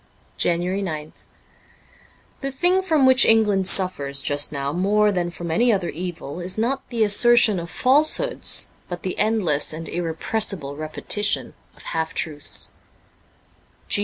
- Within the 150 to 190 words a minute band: No, slow, 135 wpm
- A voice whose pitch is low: No, medium, 185 Hz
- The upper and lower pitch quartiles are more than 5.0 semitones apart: Yes, wide, 5.6 semitones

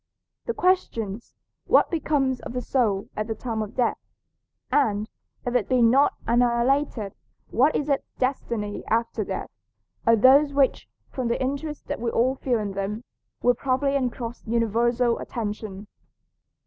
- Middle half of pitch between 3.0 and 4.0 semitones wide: Yes, average, 3.3 semitones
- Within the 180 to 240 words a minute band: No, average, 150 wpm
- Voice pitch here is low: No, high, 240 Hz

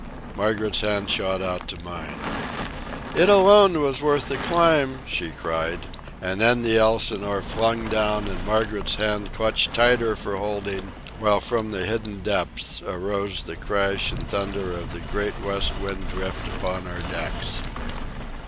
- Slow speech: No, average, 150 wpm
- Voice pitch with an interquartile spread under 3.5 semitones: Yes, average, 3.0 semitones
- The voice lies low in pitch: Yes, low, 100 Hz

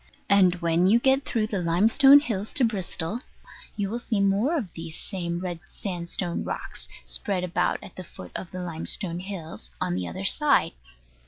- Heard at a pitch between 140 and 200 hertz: Yes, high, 190 Hz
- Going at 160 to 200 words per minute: Yes, average, 175 wpm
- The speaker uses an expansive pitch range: No, average, 4.1 semitones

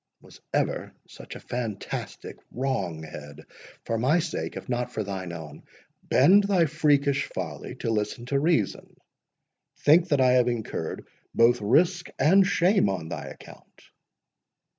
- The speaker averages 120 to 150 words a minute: Yes, average, 140 wpm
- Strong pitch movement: Yes, wide, 7.1 semitones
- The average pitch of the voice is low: Yes, low, 125 Hz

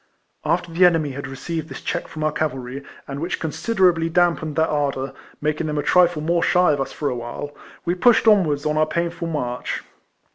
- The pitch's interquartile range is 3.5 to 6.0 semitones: No, average, 3.1 semitones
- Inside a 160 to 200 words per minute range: Yes, average, 195 wpm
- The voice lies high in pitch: No, medium, 155 Hz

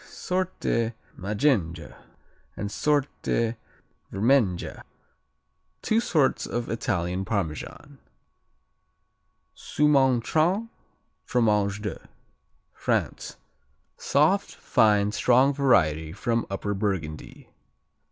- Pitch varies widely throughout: Yes, wide, 5.7 semitones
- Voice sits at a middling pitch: No, low, 110 Hz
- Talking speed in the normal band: No, slow, 70 wpm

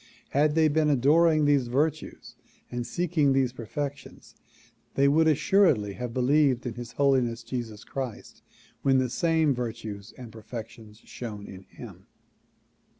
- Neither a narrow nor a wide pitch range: Yes, average, 4.1 semitones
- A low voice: Yes, low, 130 Hz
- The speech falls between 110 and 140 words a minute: Yes, slow, 135 wpm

